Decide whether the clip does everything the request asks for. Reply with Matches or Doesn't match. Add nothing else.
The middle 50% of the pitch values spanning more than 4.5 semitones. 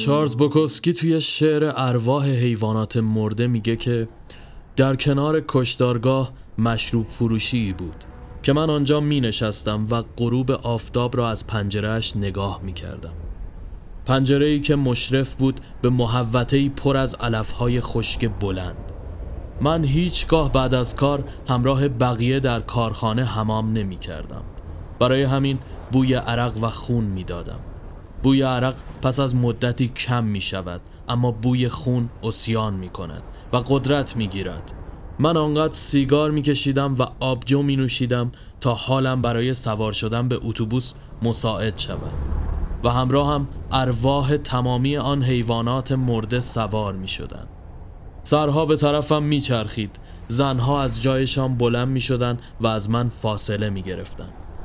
Doesn't match